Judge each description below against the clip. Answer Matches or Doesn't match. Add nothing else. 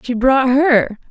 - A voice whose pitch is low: Doesn't match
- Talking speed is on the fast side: Doesn't match